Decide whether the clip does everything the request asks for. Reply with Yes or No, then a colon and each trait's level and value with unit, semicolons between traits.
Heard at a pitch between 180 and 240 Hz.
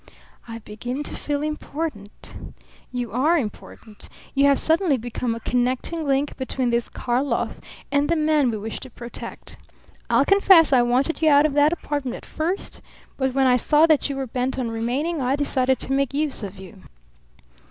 No: very high, 270 Hz